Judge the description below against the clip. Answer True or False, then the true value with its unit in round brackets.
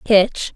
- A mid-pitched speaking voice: False (205 Hz)